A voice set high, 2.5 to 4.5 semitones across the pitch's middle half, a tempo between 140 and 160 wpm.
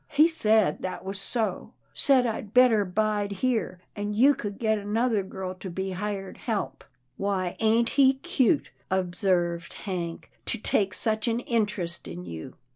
No: high, 205 Hz; average, 3.7 semitones; average, 170 wpm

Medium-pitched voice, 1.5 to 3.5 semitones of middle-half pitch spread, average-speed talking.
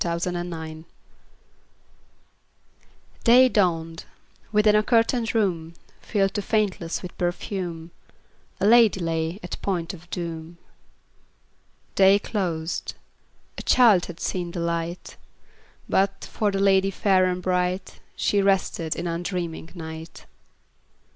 No: medium, 180 Hz; average, 3.0 semitones; slow, 125 wpm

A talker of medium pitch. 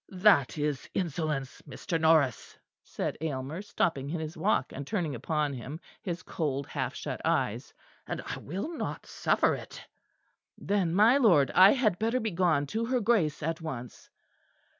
Yes: medium, 160 Hz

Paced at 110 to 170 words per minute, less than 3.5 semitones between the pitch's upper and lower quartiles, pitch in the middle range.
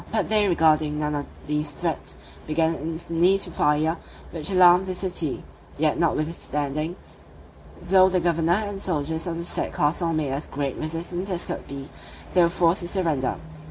Yes: average, 165 wpm; average, 2.8 semitones; medium, 165 Hz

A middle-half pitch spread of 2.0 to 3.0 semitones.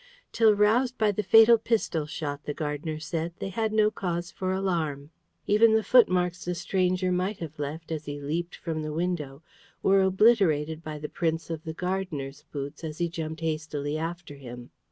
No: average, 4.0 semitones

